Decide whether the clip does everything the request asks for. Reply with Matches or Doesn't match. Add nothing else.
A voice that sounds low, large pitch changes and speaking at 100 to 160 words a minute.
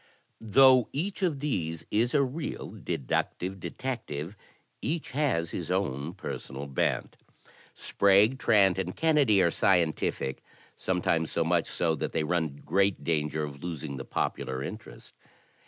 Matches